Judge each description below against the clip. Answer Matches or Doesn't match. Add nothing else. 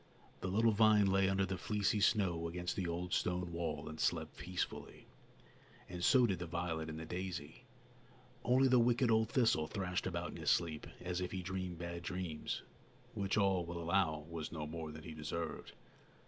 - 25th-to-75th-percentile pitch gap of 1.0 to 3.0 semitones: Matches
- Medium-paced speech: Matches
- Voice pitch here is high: Doesn't match